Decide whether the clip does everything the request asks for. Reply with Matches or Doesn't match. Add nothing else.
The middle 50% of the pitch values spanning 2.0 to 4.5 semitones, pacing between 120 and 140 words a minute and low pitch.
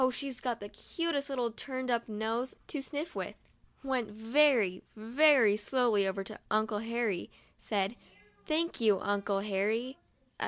Doesn't match